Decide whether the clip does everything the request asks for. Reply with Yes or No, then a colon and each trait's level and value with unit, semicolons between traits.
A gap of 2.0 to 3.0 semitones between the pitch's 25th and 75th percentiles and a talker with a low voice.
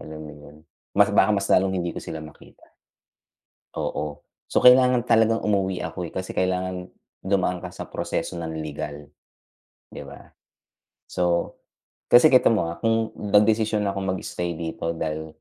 No: average, 4.3 semitones; very low, 95 Hz